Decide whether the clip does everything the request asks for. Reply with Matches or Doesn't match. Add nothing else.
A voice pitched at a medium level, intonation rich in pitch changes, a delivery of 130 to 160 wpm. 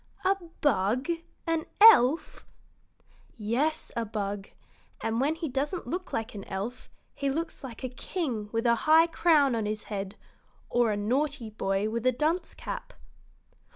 Doesn't match